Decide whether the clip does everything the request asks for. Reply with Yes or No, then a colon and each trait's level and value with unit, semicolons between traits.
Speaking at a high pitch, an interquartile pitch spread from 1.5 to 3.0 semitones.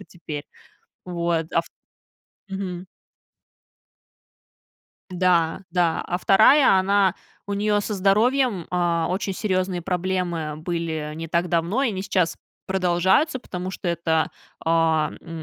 No: medium, 180 Hz; narrow, 2.6 semitones